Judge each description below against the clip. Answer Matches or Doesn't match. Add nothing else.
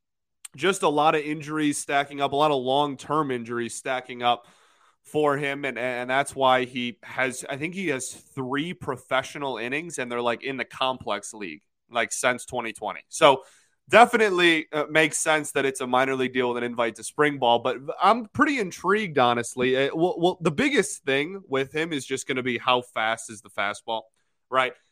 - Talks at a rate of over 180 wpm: Matches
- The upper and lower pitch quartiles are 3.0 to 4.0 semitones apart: Matches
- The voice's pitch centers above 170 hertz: Doesn't match